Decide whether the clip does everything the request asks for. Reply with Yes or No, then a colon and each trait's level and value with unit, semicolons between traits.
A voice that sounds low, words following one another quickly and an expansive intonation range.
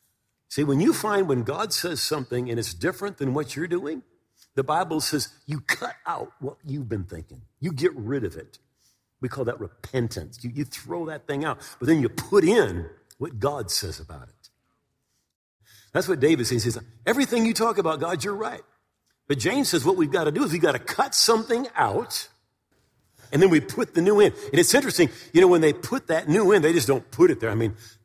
No: medium, 150 Hz; fast, 220 wpm; wide, 8.2 semitones